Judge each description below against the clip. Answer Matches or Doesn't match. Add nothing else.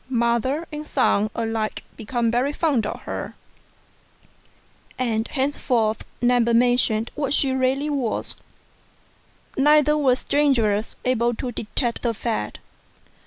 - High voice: Matches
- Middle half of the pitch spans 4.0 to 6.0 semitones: Doesn't match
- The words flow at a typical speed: Doesn't match